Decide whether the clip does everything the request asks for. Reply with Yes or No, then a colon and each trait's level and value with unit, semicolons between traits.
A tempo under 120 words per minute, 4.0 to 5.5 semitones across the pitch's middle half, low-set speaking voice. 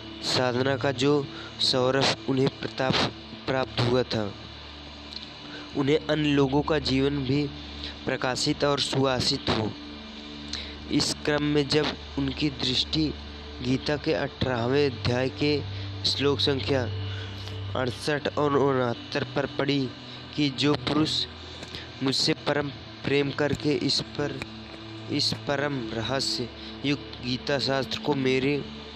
Yes: slow, 110 wpm; average, 4.7 semitones; low, 130 Hz